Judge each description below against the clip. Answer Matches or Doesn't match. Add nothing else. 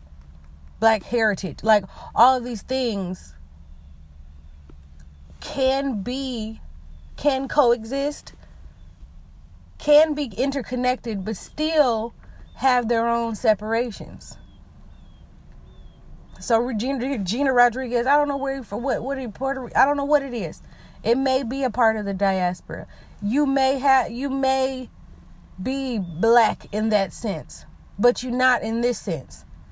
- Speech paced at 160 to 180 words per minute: Doesn't match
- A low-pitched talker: Doesn't match